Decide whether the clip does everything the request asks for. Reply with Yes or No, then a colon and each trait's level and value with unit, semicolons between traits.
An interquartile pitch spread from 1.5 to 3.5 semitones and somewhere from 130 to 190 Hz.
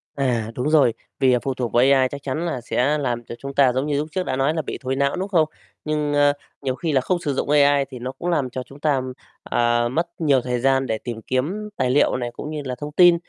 Yes: average, 2.8 semitones; low, 135 Hz